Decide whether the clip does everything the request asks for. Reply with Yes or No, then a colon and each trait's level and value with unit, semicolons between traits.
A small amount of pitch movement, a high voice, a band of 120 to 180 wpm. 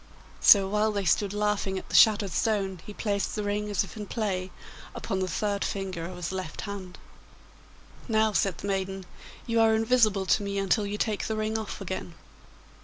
No: narrow, 2.0 semitones; high, 200 Hz; average, 190 wpm